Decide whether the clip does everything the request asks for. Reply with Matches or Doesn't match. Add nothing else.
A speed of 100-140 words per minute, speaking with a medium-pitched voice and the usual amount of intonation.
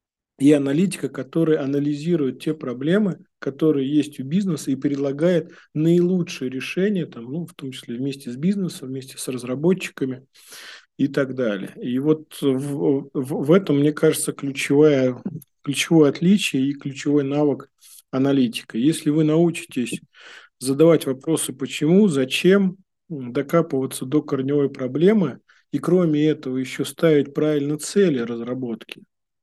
Matches